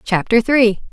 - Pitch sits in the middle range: No, high, 225 Hz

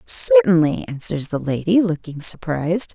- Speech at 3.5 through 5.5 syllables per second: Yes, 4.6 syllables/s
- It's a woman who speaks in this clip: Yes, female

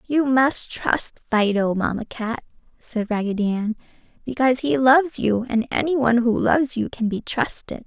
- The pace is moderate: Yes, average, 160 wpm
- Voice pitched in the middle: No, high, 240 Hz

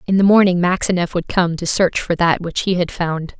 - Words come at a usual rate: No, fast, 245 wpm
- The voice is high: No, medium, 175 Hz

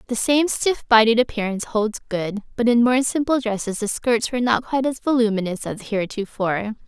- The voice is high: Yes, high, 230 Hz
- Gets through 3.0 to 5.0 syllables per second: No, 5.7 syllables/s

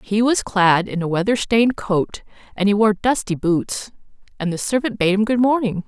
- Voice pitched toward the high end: Yes, high, 205 Hz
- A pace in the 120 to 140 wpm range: No, fast, 205 wpm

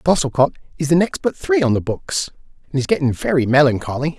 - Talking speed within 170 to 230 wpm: Yes, average, 200 wpm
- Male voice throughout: Yes, male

